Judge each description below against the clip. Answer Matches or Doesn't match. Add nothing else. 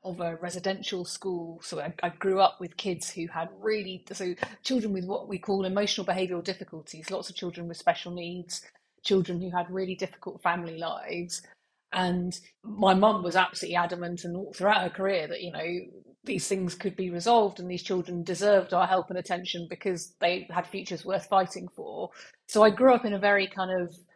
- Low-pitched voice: Doesn't match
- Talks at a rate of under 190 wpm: Doesn't match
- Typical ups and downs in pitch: Doesn't match